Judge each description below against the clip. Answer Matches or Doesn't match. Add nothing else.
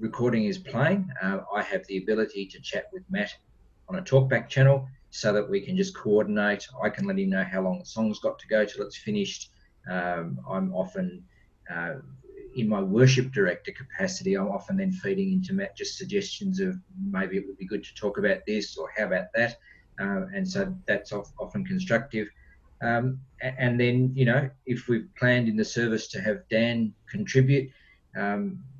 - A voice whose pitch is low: Matches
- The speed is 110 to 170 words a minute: Doesn't match